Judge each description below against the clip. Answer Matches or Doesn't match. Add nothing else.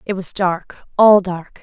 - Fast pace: Doesn't match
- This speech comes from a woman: Matches